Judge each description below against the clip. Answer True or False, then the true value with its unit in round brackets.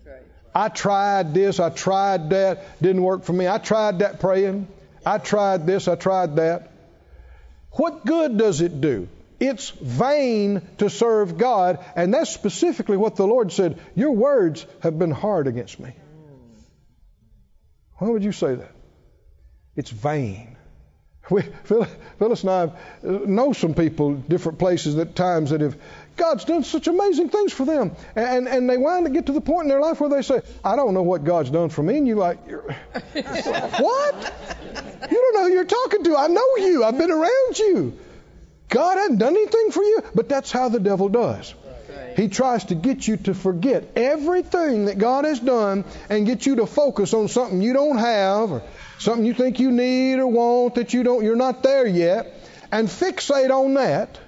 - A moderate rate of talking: True (185 wpm)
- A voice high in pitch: True (210 Hz)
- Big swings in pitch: True (7.1 semitones)